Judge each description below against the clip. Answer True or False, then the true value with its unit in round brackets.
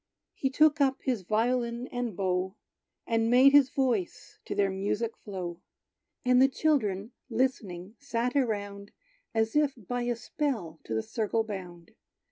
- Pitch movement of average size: True (4.6 semitones)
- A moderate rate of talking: True (145 wpm)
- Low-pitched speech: False (225 Hz)